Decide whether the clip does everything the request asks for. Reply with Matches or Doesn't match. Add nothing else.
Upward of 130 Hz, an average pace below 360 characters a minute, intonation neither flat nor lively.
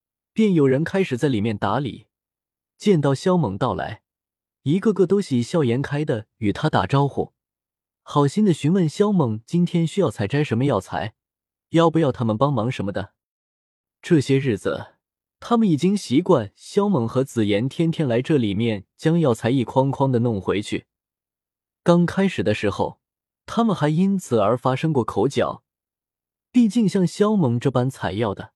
Doesn't match